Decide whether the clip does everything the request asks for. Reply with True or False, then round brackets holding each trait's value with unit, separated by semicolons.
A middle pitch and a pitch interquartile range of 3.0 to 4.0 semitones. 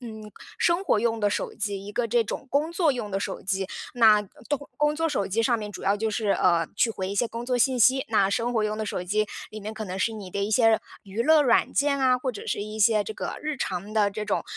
False (220 Hz; 3.5 semitones)